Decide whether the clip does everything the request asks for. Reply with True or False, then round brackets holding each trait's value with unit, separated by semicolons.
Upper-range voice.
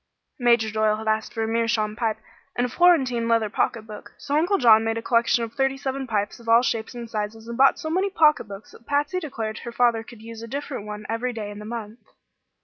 True (230 Hz)